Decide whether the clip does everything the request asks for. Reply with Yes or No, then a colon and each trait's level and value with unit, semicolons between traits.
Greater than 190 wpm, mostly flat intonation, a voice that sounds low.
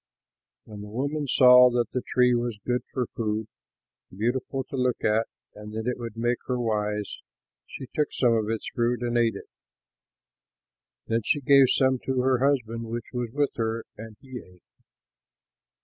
No: average, 170 wpm; narrow, 2.3 semitones; low, 120 Hz